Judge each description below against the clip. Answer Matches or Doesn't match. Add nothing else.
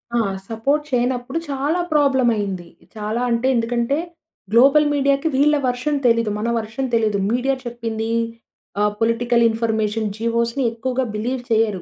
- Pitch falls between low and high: Doesn't match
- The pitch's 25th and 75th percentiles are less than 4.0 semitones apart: Matches